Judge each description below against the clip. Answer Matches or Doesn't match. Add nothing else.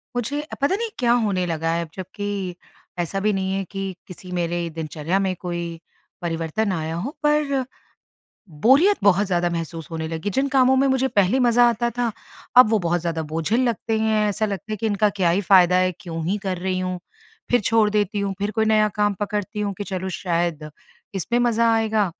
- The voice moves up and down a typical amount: Matches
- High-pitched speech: Matches